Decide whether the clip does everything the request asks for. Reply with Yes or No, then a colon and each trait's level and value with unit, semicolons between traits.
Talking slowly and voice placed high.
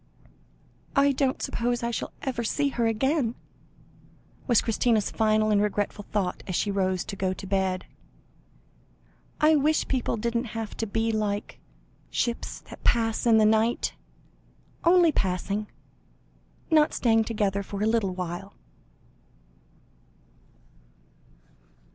Yes: slow, 125 wpm; high, 220 Hz